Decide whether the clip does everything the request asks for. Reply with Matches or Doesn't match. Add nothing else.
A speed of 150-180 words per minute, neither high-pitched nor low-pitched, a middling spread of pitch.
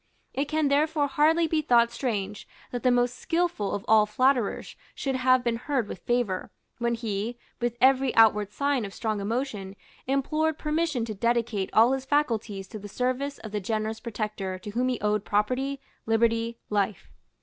Doesn't match